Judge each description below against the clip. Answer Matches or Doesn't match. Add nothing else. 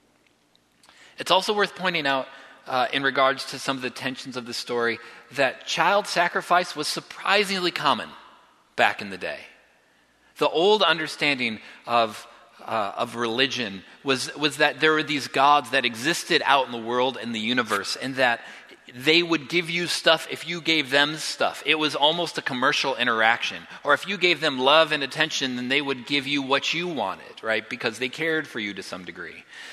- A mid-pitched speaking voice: Matches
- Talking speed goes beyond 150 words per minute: Matches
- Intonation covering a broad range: Doesn't match